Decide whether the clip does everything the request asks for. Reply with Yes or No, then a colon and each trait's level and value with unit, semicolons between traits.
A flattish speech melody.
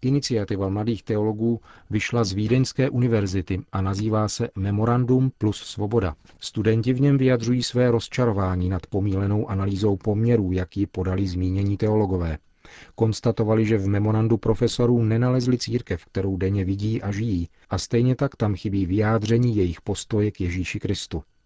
No: average, 3.2 semitones